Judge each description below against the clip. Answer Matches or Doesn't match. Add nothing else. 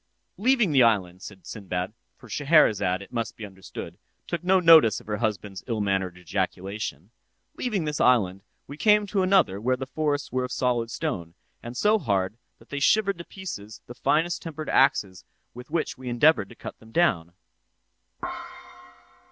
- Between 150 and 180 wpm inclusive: Matches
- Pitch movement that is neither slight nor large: Doesn't match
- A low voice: Matches